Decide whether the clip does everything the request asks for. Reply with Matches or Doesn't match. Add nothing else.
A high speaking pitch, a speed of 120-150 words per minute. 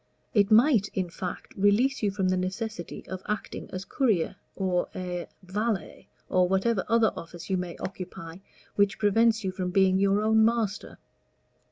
Doesn't match